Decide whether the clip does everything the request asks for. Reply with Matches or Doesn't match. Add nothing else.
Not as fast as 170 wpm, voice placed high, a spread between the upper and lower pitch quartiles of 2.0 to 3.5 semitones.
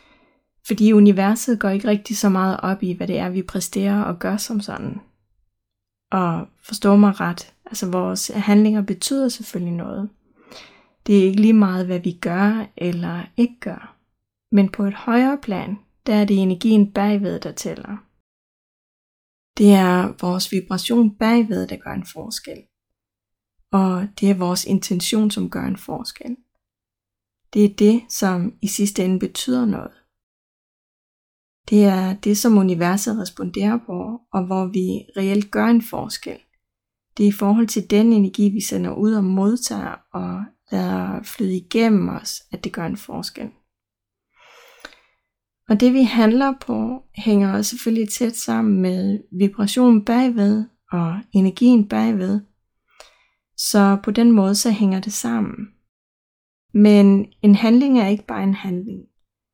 Matches